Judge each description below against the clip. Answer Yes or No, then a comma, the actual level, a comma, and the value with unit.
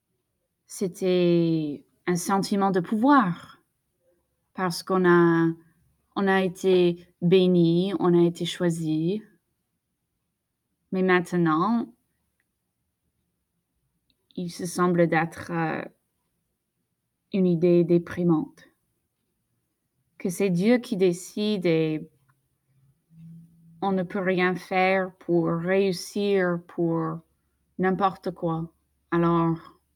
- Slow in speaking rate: Yes, slow, 85 wpm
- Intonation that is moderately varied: No, narrow, 2.2 semitones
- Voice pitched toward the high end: No, medium, 175 Hz